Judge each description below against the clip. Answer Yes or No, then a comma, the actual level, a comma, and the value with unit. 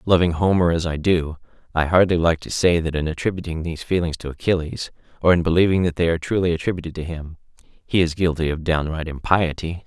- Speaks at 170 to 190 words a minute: No, average, 200 wpm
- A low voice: Yes, very low, 85 Hz